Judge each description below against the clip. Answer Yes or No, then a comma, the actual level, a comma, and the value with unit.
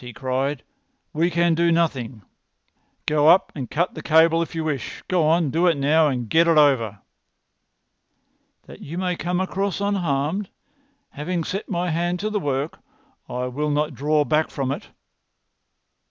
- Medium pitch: Yes, medium, 160 Hz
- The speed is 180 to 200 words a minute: No, average, 160 wpm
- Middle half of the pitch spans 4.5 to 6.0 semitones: No, average, 3.7 semitones